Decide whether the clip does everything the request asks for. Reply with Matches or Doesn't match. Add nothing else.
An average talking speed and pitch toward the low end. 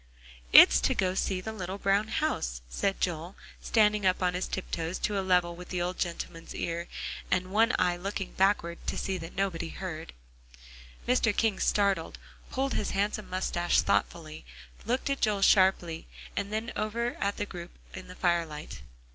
Doesn't match